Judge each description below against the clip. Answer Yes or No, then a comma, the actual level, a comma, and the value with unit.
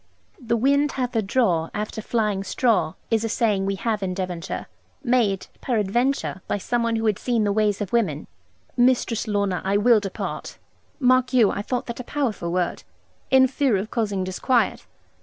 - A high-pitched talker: Yes, high, 220 Hz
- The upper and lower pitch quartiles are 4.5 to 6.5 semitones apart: No, average, 3.9 semitones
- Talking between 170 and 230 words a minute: Yes, average, 175 wpm